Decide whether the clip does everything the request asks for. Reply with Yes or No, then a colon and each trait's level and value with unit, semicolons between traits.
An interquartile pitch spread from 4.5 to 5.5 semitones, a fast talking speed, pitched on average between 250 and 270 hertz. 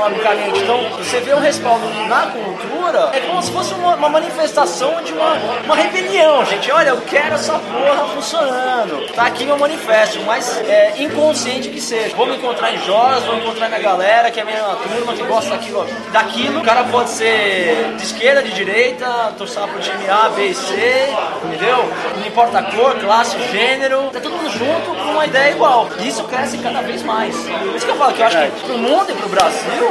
Yes: average, 5.0 semitones; fast, 205 wpm; very high, 255 Hz